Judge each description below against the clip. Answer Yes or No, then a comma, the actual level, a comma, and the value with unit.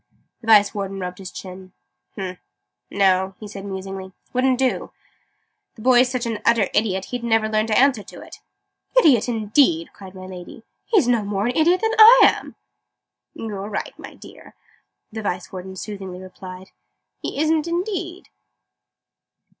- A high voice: Yes, high, 210 Hz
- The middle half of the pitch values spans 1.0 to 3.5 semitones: No, average, 5.0 semitones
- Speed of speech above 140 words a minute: Yes, average, 160 wpm